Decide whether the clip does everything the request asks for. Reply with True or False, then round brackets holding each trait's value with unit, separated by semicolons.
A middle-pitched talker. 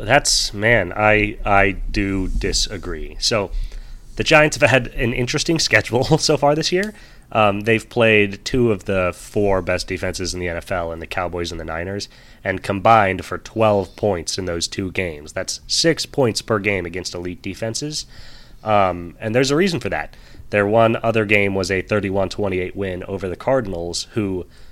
False (100 Hz)